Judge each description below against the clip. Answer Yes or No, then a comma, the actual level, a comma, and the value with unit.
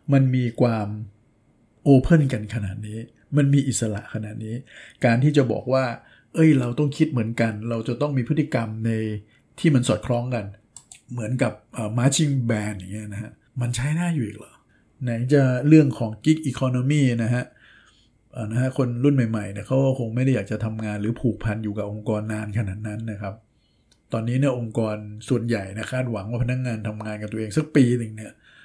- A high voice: No, low, 120 Hz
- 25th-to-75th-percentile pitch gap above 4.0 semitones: No, average, 3.4 semitones